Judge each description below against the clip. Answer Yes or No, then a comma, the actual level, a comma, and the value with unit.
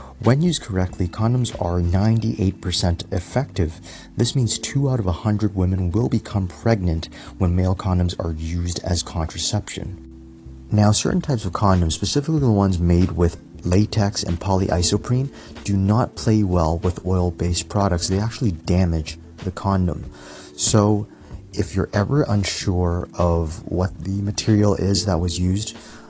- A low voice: Yes, very low, 95 Hz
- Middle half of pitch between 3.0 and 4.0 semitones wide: Yes, average, 3.5 semitones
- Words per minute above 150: No, average, 145 wpm